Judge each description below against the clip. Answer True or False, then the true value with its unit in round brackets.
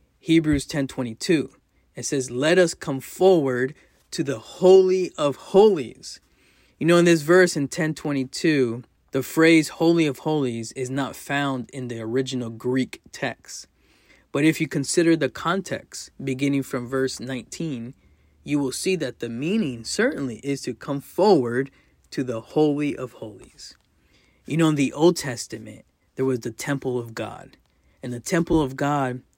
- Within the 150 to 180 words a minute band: True (155 wpm)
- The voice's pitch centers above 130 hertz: True (140 Hz)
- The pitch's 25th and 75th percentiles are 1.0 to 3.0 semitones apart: False (4.1 semitones)